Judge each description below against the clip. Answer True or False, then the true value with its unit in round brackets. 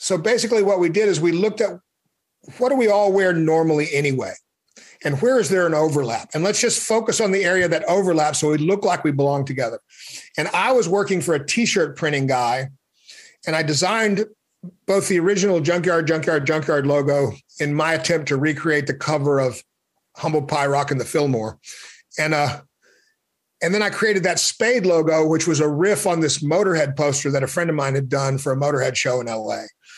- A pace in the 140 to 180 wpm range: False (200 wpm)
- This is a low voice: False (160 Hz)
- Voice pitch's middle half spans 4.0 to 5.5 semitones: True (5.1 semitones)